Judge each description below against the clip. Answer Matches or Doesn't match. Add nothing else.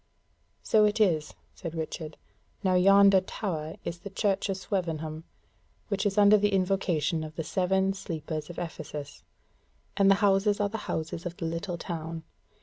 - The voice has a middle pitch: Matches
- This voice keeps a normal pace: Matches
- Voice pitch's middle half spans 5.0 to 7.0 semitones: Doesn't match